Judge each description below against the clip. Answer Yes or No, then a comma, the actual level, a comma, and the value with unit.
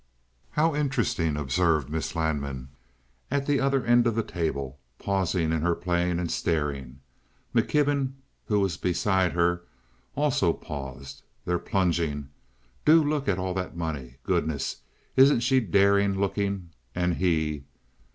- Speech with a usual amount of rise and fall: No, wide, 6.1 semitones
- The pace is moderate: No, slow, 130 wpm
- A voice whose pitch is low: Yes, very low, 90 Hz